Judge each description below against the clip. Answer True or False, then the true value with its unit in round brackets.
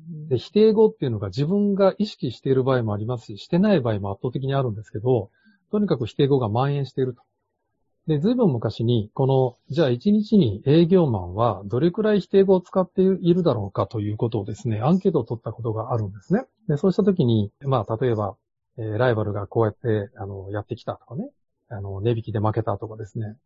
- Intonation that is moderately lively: False (7.9 semitones)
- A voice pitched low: True (125 Hz)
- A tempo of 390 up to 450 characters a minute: True (440 characters per minute)